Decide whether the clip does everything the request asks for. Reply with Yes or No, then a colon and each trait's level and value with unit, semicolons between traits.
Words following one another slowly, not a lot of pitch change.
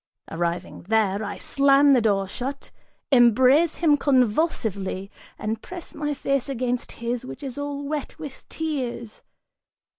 No: slow, 130 wpm; average, 4.6 semitones